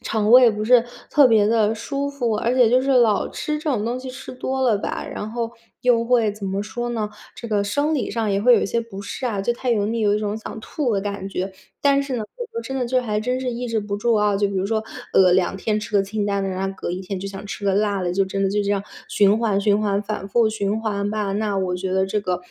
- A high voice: Yes, high, 215 Hz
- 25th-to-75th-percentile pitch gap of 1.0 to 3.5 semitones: Yes, average, 3.1 semitones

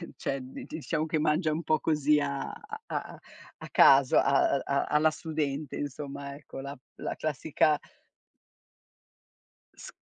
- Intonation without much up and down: Yes, narrow, 1.9 semitones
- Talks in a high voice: No, medium, 150 Hz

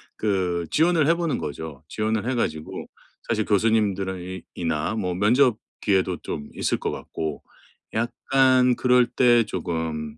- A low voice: Yes, low, 105 Hz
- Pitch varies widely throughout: Yes, wide, 6.2 semitones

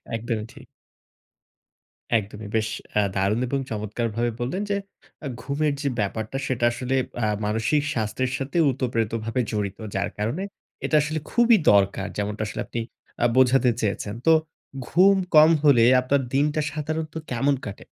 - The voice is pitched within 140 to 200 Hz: No, low, 120 Hz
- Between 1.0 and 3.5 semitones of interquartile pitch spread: No, average, 5.0 semitones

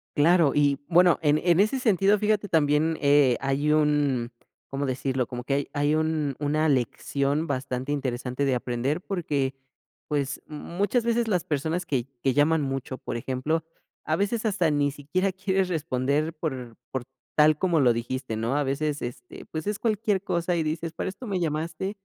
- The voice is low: No, medium, 150 Hz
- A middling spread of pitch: Yes, average, 4.3 semitones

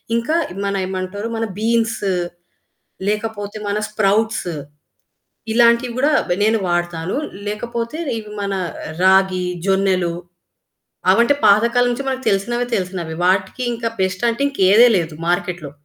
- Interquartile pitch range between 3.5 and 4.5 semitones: Yes, average, 3.8 semitones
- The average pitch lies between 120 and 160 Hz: No, high, 205 Hz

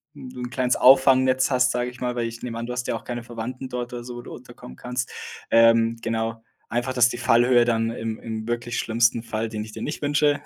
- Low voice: Yes, low, 120 Hz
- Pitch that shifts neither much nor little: No, narrow, 1.6 semitones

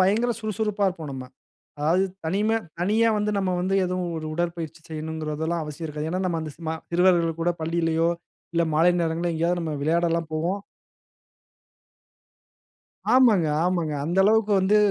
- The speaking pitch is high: No, medium, 170 Hz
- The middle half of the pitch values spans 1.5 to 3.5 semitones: Yes, average, 2.9 semitones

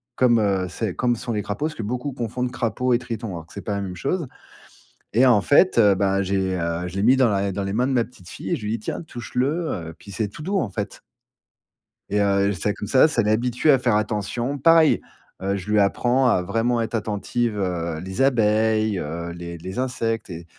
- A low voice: Yes, low, 110 Hz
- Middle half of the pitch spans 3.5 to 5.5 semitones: Yes, average, 4.2 semitones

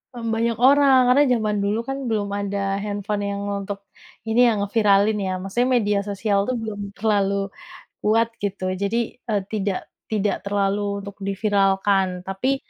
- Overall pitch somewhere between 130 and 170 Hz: No, high, 205 Hz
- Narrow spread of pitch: Yes, narrow, 1.9 semitones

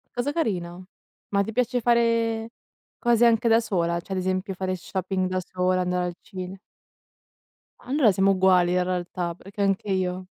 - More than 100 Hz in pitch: Yes, high, 190 Hz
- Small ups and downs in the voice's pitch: No, average, 3.6 semitones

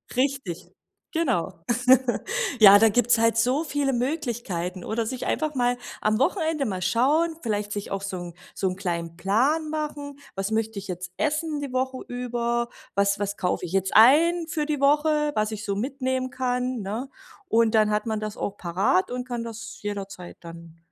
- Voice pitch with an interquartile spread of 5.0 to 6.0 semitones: Yes, wide, 5.6 semitones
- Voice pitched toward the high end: Yes, high, 230 Hz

